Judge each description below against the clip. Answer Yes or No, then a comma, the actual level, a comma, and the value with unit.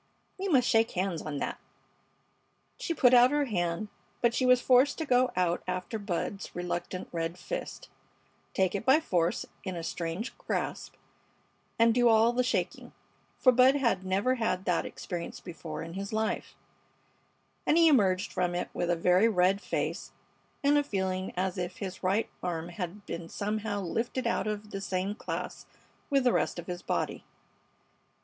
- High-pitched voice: Yes, high, 195 Hz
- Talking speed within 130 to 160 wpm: No, average, 170 wpm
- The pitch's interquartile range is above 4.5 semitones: Yes, average, 5.3 semitones